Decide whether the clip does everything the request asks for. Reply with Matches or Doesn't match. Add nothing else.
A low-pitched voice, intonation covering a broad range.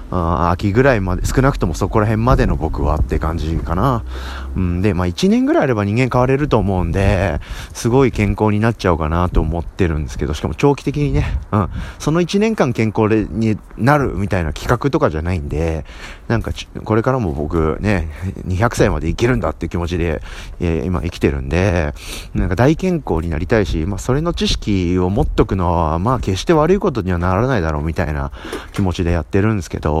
Matches